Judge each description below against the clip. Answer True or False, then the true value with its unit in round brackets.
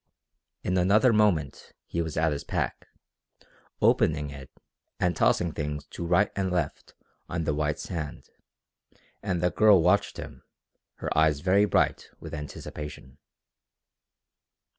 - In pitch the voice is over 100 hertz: False (85 Hz)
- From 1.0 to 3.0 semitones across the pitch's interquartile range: False (3.8 semitones)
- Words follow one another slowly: True (130 wpm)